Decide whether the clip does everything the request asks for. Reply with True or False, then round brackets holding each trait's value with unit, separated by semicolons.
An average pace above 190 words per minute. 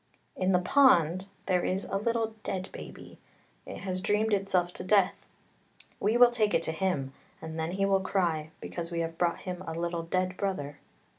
True (200 wpm)